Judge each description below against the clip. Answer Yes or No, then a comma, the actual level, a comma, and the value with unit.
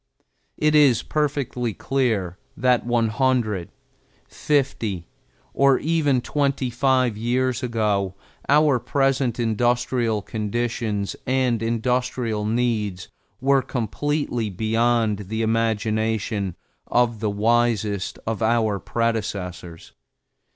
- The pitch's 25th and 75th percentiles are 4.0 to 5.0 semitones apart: No, average, 3.2 semitones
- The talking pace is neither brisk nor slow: No, slow, 95 wpm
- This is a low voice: Yes, low, 115 Hz